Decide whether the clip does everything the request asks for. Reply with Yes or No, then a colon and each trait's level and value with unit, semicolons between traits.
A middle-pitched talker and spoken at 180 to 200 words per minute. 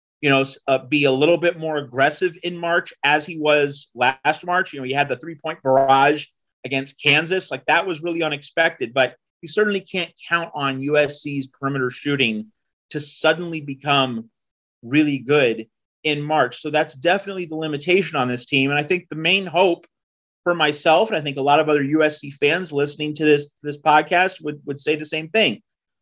Yes: medium, 150 Hz; average, 190 wpm